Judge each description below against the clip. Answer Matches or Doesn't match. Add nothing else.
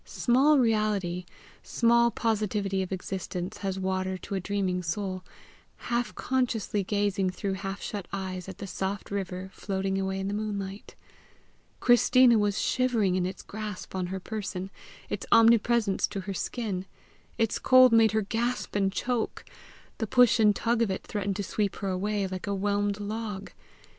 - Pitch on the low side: Doesn't match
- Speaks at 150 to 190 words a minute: Matches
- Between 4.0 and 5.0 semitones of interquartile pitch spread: Doesn't match